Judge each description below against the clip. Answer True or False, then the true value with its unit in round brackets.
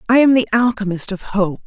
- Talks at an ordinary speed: False (215 wpm)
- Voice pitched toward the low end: False (215 Hz)